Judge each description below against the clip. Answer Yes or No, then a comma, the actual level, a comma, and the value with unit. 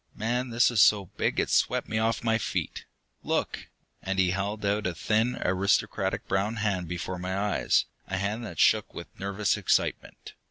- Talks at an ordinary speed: Yes, average, 175 wpm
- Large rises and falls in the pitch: No, narrow, 2.6 semitones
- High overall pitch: No, low, 100 Hz